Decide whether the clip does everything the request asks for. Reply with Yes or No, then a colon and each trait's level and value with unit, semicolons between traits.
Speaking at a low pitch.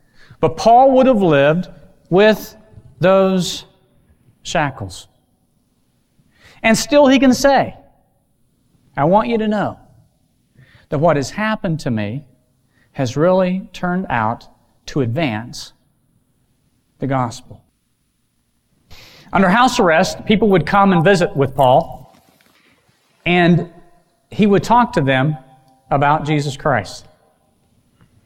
No: medium, 160 Hz